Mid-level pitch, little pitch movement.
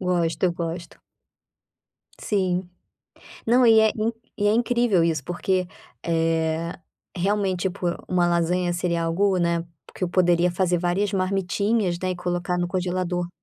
Yes: medium, 180 Hz; narrow, 2.1 semitones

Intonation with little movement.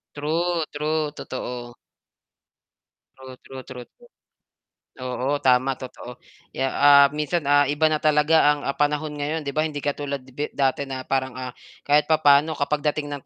Yes: narrow, 2.3 semitones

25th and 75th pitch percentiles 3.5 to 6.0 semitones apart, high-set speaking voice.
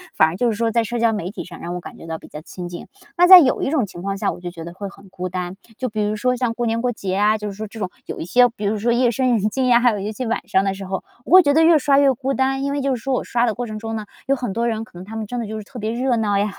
Yes: average, 4.1 semitones; high, 225 Hz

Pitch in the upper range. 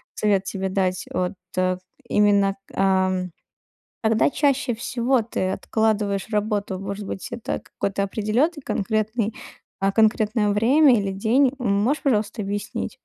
Yes: high, 210 Hz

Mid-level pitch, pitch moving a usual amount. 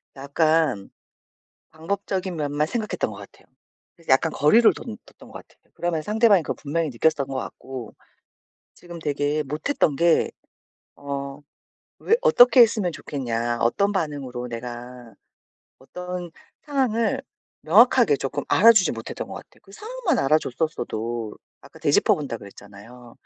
No: medium, 155 Hz; wide, 7.0 semitones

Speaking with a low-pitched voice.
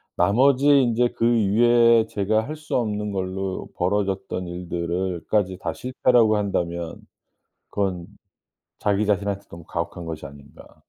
Yes: low, 100 Hz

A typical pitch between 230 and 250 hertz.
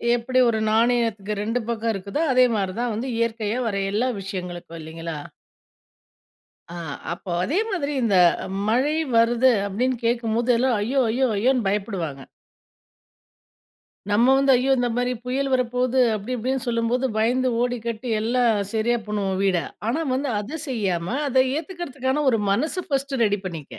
Yes: high, 235 Hz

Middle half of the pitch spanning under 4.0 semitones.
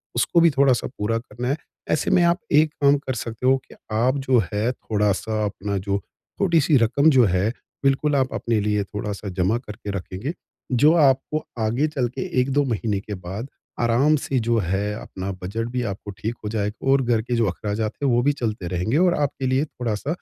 No: average, 4.7 semitones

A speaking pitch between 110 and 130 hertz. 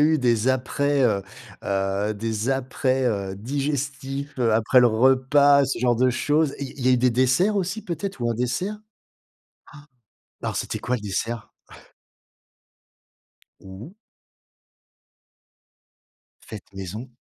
Yes: low, 125 Hz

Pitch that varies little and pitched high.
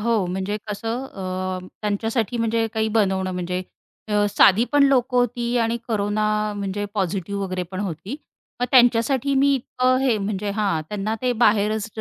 No: average, 3.3 semitones; high, 210 Hz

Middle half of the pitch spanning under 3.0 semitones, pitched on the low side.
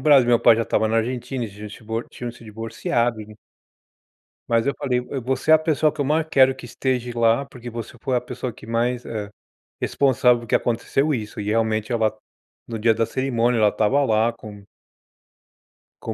Yes: narrow, 2.6 semitones; low, 120 Hz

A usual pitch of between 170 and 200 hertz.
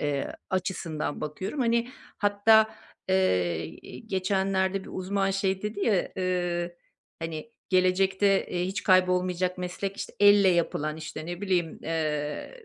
Yes: medium, 185 Hz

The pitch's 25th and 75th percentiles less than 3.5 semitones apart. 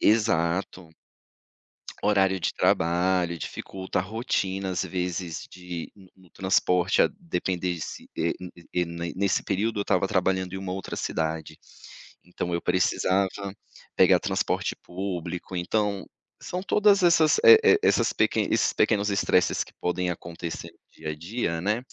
Yes: narrow, 2.4 semitones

